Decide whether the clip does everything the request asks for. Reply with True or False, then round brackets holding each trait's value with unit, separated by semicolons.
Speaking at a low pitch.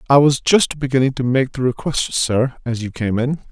True (130 Hz)